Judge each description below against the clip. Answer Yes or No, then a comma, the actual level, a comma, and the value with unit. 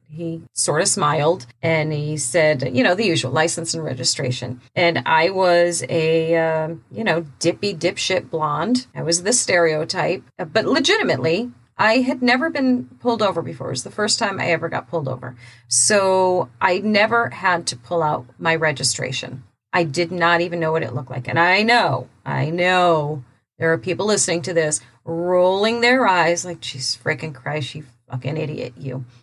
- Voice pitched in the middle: Yes, medium, 165 Hz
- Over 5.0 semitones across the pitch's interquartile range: Yes, wide, 5.5 semitones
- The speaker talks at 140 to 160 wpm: No, average, 180 wpm